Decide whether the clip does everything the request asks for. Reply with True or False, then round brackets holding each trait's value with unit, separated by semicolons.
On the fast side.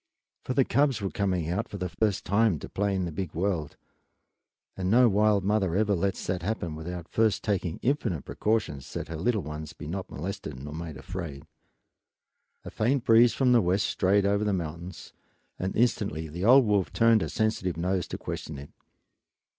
False (185 wpm)